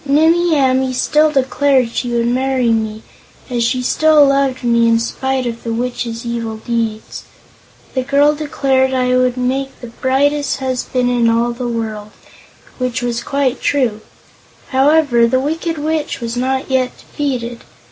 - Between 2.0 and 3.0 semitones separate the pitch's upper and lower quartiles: Yes, average, 2.7 semitones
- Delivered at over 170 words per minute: No, average, 150 wpm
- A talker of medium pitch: No, very high, 255 Hz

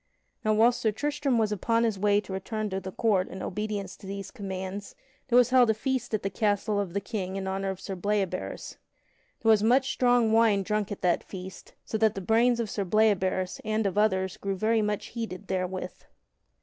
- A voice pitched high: Yes, high, 210 Hz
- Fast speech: Yes, fast, 210 wpm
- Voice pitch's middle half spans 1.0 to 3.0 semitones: Yes, average, 2.7 semitones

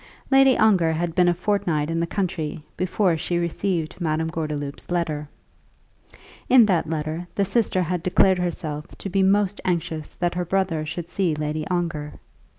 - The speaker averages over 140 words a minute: Yes, average, 160 wpm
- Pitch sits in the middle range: Yes, medium, 175 Hz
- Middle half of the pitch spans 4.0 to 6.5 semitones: No, average, 3.0 semitones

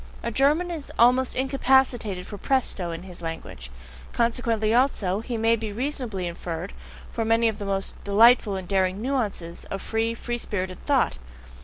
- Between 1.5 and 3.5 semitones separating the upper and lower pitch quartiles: No, average, 4.6 semitones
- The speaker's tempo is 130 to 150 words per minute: No, average, 160 wpm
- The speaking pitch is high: Yes, high, 225 Hz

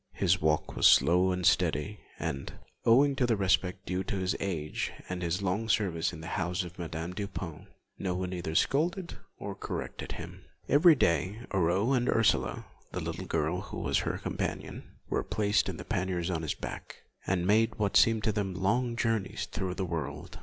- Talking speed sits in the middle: Yes, average, 180 wpm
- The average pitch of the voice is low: Yes, very low, 95 Hz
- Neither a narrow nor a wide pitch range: Yes, average, 3.6 semitones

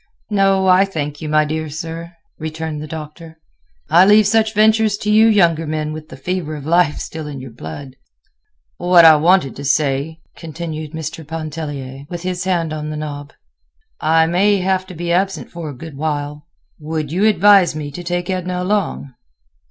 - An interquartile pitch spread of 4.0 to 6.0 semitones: No, average, 3.3 semitones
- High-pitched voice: No, medium, 160 Hz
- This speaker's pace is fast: No, average, 175 wpm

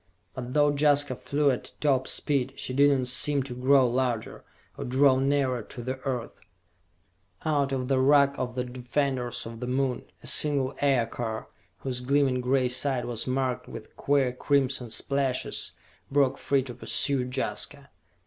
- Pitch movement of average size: No, narrow, 2.0 semitones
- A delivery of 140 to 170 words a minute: Yes, average, 160 wpm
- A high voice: No, low, 130 Hz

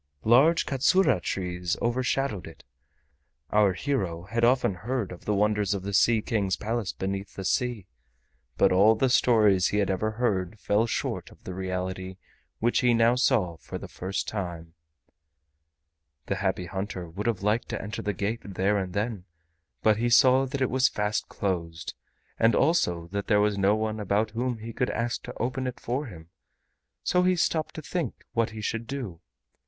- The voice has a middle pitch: No, low, 105 Hz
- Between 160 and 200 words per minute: Yes, average, 180 wpm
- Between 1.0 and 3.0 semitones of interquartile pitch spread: No, average, 4.2 semitones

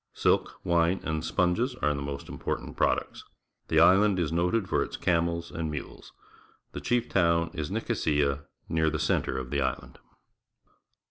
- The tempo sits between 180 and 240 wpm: No, average, 155 wpm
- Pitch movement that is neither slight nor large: Yes, average, 3.2 semitones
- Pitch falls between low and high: No, very low, 85 Hz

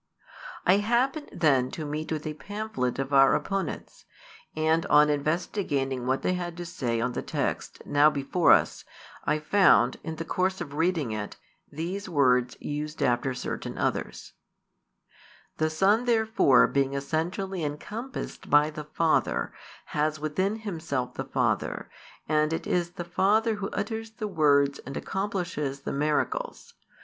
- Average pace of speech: Yes, average, 145 wpm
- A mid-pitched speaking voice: Yes, medium, 155 Hz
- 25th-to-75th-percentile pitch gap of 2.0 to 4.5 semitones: No, average, 5.2 semitones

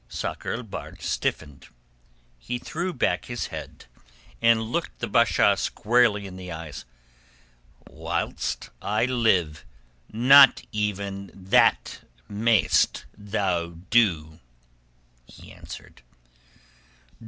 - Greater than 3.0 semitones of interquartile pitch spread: Yes, average, 4.5 semitones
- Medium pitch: No, low, 105 Hz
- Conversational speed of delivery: No, slow, 95 wpm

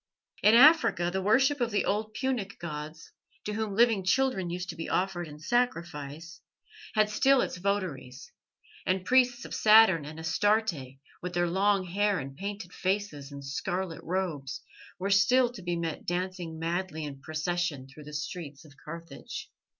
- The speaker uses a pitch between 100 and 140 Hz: No, medium, 180 Hz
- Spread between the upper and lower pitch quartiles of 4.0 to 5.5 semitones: Yes, average, 4.5 semitones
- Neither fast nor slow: Yes, average, 160 wpm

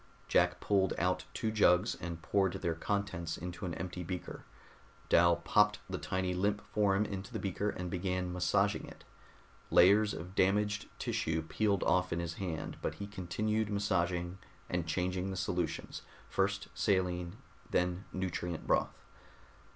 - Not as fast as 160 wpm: Yes, average, 145 wpm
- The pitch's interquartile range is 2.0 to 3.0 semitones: Yes, narrow, 2.4 semitones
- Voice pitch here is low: Yes, very low, 90 Hz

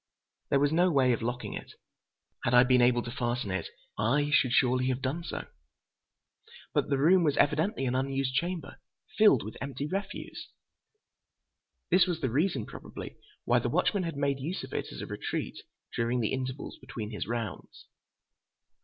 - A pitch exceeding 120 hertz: Yes, low, 135 Hz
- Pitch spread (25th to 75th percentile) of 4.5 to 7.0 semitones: No, average, 4.1 semitones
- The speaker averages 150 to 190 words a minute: Yes, average, 170 wpm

